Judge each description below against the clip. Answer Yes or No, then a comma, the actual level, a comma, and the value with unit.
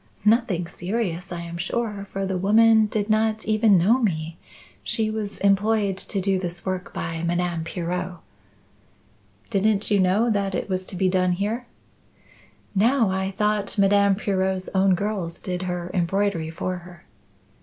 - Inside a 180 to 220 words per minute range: No, average, 155 wpm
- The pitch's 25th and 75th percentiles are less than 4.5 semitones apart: Yes, average, 2.8 semitones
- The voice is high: Yes, high, 195 Hz